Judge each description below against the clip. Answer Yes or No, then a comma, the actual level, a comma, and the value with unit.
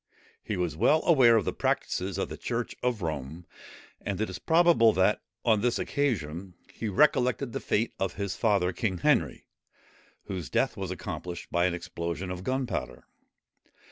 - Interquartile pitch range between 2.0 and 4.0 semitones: No, average, 5.1 semitones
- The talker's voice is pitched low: Yes, low, 100 Hz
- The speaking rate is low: No, average, 165 wpm